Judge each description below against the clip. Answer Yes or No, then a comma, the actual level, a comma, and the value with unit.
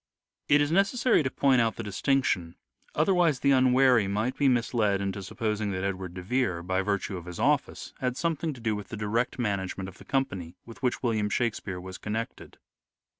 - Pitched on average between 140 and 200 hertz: No, low, 110 Hz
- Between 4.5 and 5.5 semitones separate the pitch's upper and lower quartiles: Yes, average, 5.2 semitones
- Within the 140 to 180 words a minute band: No, average, 190 wpm